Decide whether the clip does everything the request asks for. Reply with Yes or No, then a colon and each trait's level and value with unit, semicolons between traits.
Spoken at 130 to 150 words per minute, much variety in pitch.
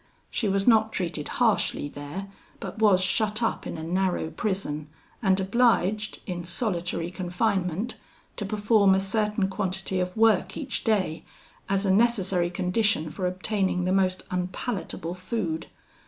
No: average, 140 wpm; average, 2.9 semitones